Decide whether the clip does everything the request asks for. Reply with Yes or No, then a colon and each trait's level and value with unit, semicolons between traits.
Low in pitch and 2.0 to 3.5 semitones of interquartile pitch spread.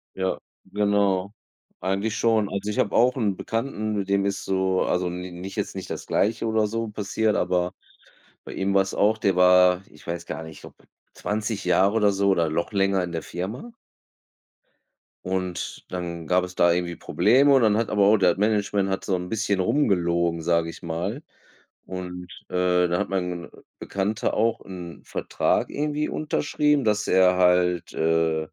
Yes: very low, 95 Hz; average, 2.9 semitones